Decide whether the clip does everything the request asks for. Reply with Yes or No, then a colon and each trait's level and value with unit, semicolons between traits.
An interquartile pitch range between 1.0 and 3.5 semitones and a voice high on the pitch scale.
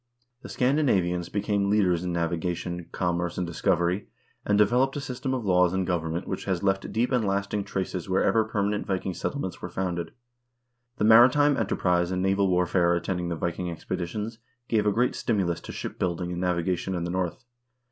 No: average, 3.2 semitones; very low, 95 Hz